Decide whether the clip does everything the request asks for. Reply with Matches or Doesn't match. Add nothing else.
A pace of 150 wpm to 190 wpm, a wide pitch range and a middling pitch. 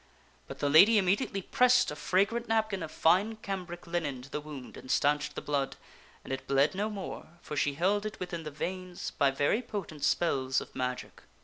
Doesn't match